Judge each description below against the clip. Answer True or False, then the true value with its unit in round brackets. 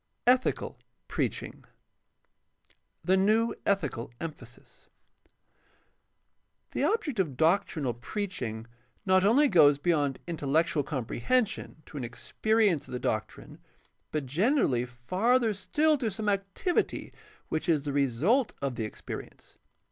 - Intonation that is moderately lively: False (8.0 semitones)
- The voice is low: False (170 Hz)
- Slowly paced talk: True (120 wpm)